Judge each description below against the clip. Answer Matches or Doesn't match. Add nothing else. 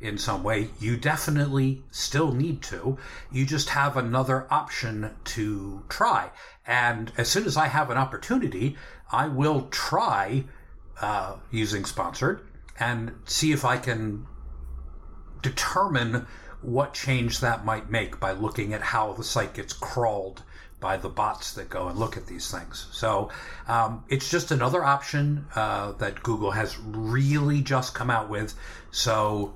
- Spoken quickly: Doesn't match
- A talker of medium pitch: Doesn't match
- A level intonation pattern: Doesn't match